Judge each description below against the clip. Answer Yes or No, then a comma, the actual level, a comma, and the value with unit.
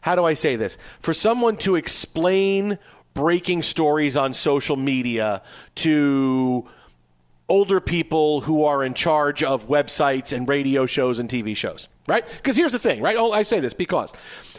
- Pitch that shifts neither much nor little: Yes, average, 4.6 semitones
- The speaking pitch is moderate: Yes, medium, 150 Hz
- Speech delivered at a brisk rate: No, average, 165 wpm